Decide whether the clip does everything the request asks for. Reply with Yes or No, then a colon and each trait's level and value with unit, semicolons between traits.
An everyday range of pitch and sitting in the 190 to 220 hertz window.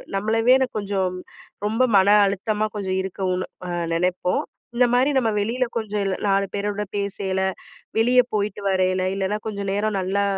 No: narrow, 2.2 semitones; high, 200 Hz